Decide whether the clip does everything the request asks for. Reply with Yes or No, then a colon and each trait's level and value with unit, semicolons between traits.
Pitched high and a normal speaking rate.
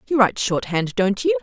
No: high, 240 Hz; fast, 210 wpm